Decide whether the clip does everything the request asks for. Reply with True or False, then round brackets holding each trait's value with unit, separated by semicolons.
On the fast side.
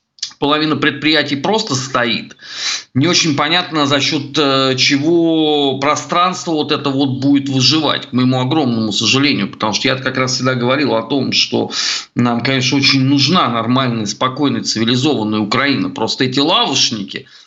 False (140 wpm)